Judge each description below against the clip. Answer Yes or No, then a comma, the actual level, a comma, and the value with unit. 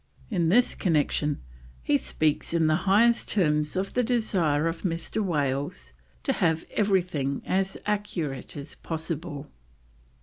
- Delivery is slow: Yes, slow, 130 wpm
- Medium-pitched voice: Yes, medium, 165 Hz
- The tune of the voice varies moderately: Yes, average, 4.6 semitones